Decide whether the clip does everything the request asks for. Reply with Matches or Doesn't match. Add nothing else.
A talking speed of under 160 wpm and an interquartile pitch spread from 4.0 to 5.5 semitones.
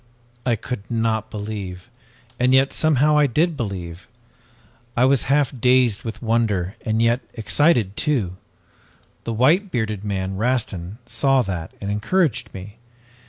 Matches